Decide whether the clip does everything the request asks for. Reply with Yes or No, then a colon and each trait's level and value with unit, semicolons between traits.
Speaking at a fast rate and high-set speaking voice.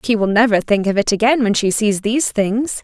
Yes: fast, 255 wpm; high, 220 Hz